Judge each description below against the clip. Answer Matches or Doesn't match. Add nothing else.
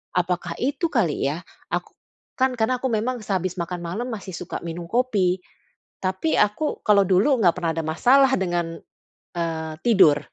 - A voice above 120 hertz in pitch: Matches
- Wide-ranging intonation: Matches